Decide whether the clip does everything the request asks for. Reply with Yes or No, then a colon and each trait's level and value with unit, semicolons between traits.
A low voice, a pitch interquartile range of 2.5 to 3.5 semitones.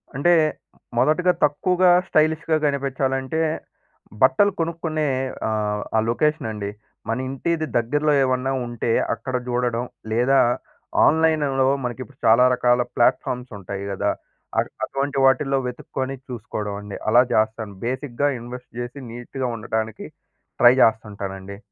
No: low, 130 Hz; average, 4.2 semitones